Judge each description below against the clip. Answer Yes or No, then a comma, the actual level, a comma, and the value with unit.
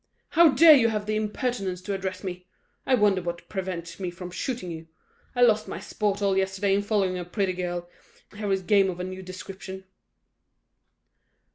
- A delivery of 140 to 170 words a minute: No, average, 180 wpm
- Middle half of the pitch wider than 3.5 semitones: No, narrow, 2.4 semitones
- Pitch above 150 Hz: Yes, high, 190 Hz